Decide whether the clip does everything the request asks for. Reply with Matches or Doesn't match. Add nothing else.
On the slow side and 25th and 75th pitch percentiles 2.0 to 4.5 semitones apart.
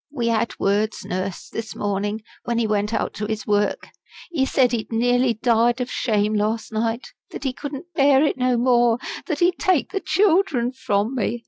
Doesn't match